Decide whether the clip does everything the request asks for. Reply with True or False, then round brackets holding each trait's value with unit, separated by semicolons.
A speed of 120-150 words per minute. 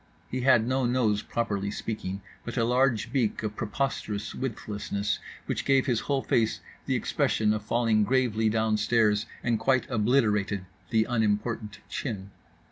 True (140 wpm)